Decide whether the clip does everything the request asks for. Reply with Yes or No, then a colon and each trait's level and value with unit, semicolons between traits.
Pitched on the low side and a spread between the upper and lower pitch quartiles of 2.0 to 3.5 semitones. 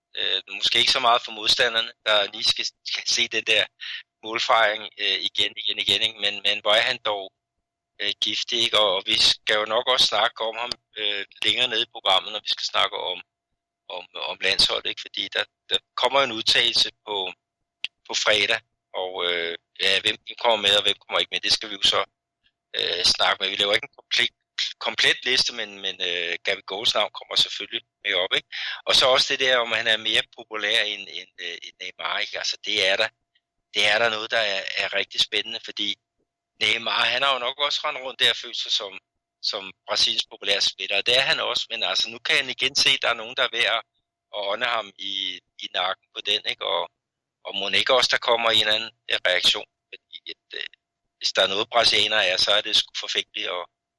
Yes: low, 110 Hz; narrow, 2.5 semitones